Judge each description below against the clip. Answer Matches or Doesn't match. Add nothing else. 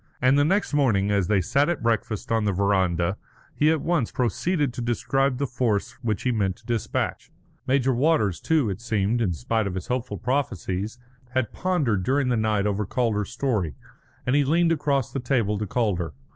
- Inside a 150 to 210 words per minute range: Matches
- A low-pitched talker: Matches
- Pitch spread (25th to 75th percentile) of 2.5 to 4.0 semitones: Doesn't match